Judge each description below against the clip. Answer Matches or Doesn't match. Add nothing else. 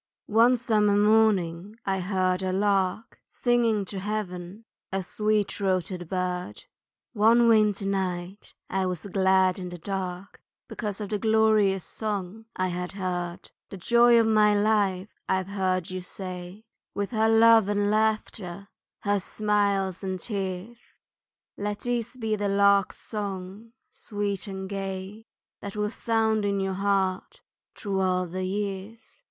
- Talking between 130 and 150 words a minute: Matches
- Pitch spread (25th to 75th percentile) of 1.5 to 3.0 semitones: Matches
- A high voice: Matches